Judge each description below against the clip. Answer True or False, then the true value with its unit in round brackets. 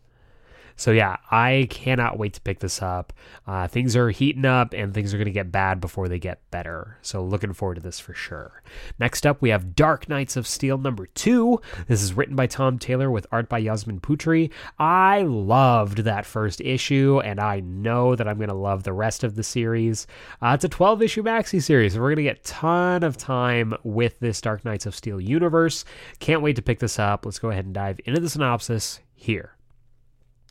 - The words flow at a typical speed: False (215 wpm)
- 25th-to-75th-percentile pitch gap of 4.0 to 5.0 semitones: True (4.7 semitones)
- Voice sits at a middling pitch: False (120 Hz)